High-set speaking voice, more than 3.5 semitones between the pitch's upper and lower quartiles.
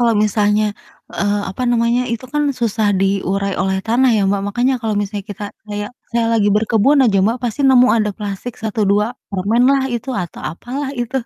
No: high, 215 Hz; average, 3.0 semitones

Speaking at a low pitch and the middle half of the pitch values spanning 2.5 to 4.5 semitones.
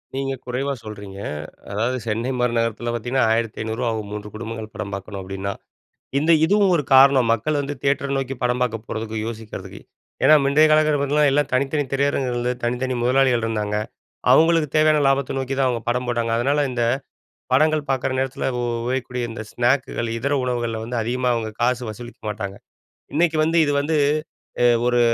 Yes: low, 125 Hz; average, 3.4 semitones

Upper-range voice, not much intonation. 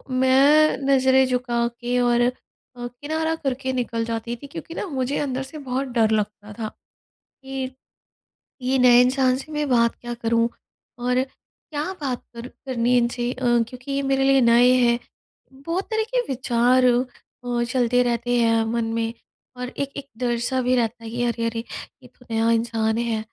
Yes: high, 245 Hz; narrow, 2.1 semitones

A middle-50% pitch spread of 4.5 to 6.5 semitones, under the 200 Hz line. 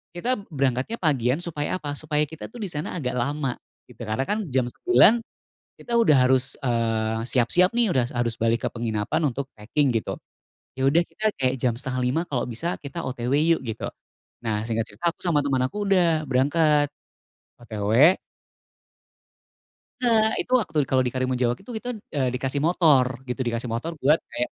Yes: average, 5.1 semitones; low, 135 Hz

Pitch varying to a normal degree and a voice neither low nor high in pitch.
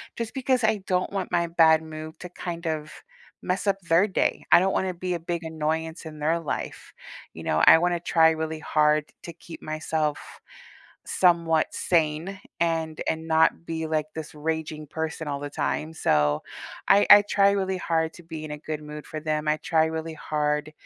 No: narrow, 2.0 semitones; medium, 160 Hz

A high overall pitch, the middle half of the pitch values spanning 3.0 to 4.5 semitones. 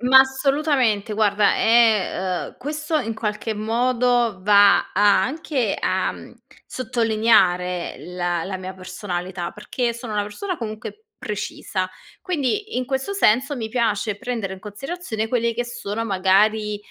Yes: high, 220 Hz; average, 4.0 semitones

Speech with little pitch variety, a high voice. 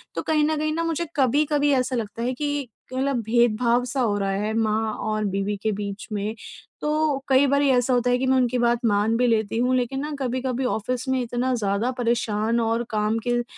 No: average, 3.2 semitones; high, 245 Hz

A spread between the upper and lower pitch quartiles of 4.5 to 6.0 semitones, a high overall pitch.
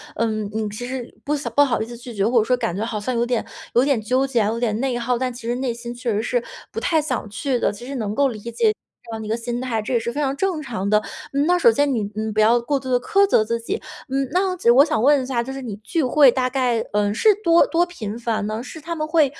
No: average, 3.7 semitones; high, 245 Hz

